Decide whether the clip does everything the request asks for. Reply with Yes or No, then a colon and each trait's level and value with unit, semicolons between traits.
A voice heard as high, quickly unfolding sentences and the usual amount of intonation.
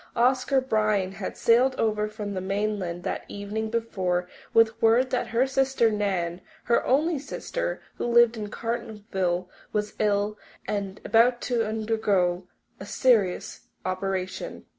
No: high, 215 Hz; slow, 135 wpm; average, 3.4 semitones